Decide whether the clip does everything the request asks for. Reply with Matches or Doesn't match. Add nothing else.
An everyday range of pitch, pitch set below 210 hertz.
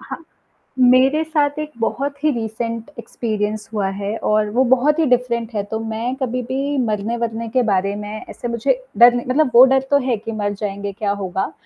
Doesn't match